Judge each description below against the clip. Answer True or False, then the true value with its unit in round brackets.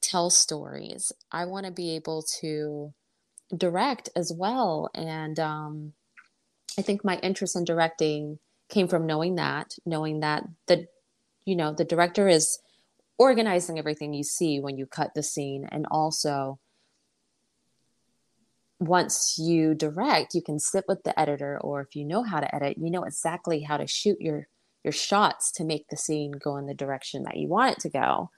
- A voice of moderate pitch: True (160 Hz)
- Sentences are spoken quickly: False (170 wpm)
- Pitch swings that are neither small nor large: True (3.1 semitones)